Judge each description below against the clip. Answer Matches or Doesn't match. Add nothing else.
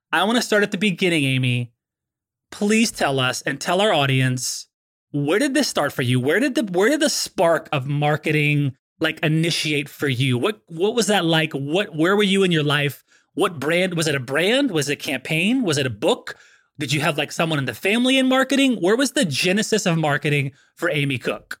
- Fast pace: Matches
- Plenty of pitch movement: Matches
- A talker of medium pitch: Matches